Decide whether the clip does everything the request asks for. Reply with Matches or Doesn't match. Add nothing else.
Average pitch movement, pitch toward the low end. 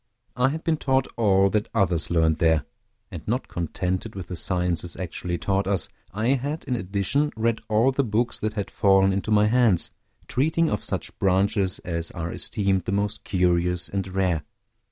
Matches